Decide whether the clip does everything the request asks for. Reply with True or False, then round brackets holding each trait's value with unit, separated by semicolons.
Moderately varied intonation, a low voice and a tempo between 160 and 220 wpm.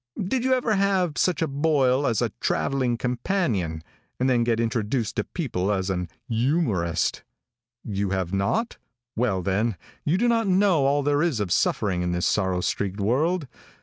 False (8.7 semitones; 125 Hz; 170 wpm)